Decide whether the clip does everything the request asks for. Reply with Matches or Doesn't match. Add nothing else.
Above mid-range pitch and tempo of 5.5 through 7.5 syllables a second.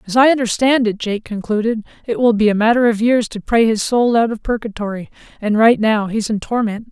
Matches